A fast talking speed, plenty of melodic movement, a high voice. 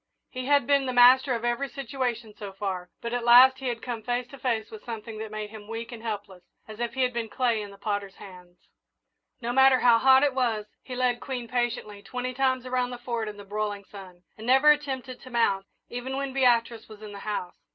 No: fast, 230 wpm; average, 3.1 semitones; high, 235 Hz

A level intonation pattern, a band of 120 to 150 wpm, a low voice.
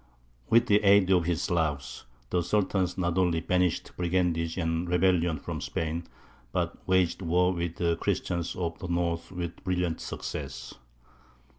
Yes: narrow, 1.6 semitones; average, 145 wpm; very low, 85 Hz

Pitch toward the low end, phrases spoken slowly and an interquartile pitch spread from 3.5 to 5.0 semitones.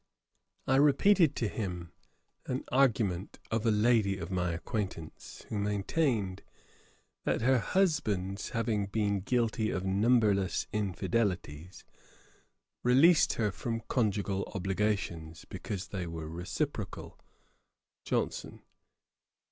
Yes: low, 105 Hz; slow, 100 wpm; average, 3.9 semitones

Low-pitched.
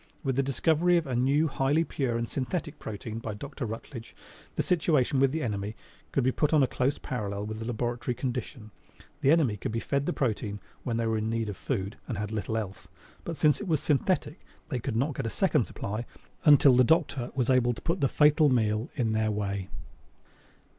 Yes: low, 125 Hz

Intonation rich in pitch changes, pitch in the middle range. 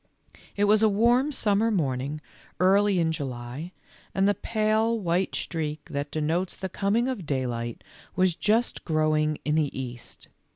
Yes: wide, 5.7 semitones; medium, 175 Hz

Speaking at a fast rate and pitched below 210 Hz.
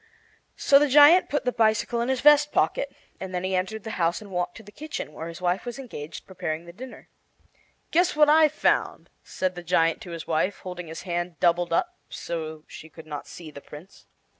Yes: fast, 215 wpm; medium, 185 Hz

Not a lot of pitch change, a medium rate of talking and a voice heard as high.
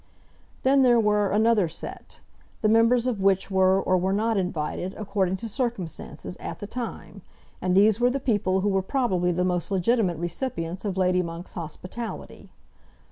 No: average, 3.9 semitones; average, 165 wpm; high, 195 Hz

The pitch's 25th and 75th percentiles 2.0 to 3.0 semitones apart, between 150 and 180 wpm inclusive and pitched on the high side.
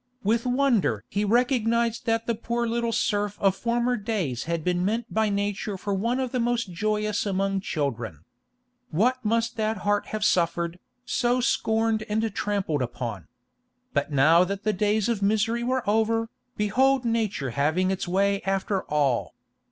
No: average, 3.8 semitones; average, 160 wpm; high, 210 Hz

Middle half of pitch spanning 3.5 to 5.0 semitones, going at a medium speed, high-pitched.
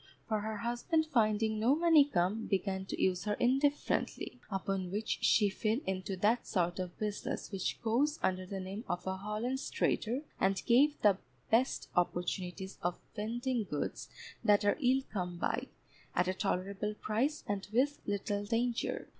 Yes: average, 4.1 semitones; average, 160 wpm; high, 210 Hz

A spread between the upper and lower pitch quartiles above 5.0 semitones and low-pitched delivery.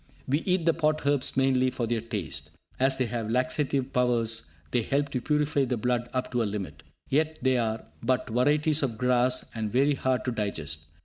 No: average, 3.4 semitones; low, 125 Hz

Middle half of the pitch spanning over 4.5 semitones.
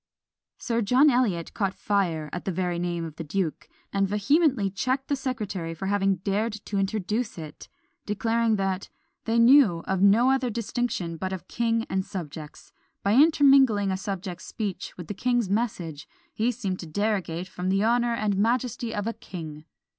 No: average, 4.1 semitones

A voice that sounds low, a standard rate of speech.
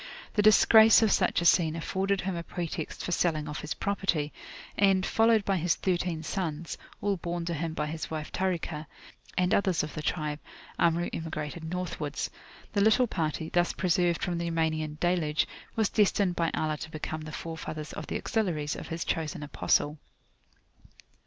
No: medium, 170 Hz; average, 170 wpm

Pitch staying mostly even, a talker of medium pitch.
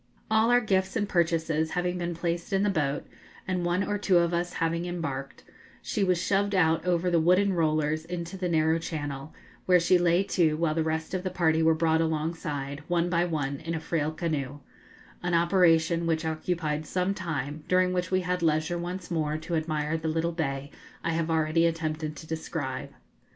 Yes: narrow, 2.1 semitones; medium, 165 Hz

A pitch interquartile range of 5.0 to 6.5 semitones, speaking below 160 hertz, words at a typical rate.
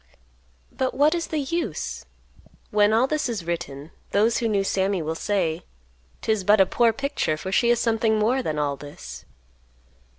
No: wide, 5.5 semitones; high, 210 Hz; average, 170 wpm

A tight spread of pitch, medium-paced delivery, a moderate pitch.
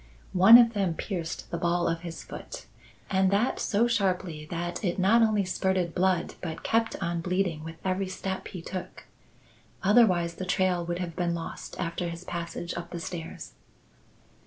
Yes: narrow, 2.1 semitones; average, 170 wpm; medium, 180 Hz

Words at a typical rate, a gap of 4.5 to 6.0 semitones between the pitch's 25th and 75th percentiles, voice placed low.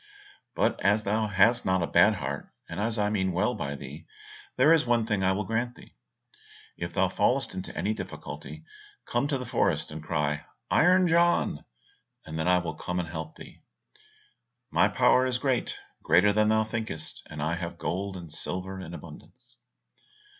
Yes: average, 180 wpm; wide, 5.4 semitones; very low, 95 Hz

